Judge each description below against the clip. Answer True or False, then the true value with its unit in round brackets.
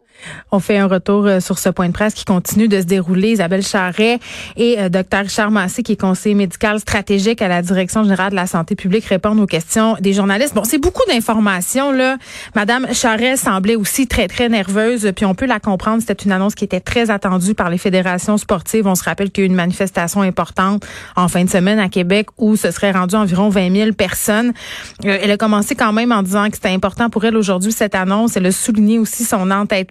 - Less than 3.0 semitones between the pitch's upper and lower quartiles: True (2.5 semitones)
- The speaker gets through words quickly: True (225 wpm)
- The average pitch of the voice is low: False (205 Hz)